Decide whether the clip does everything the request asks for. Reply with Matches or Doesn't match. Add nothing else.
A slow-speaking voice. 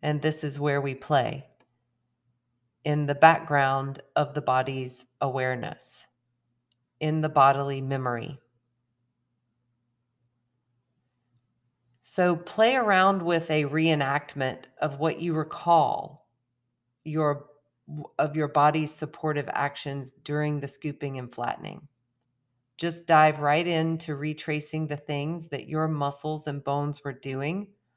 Matches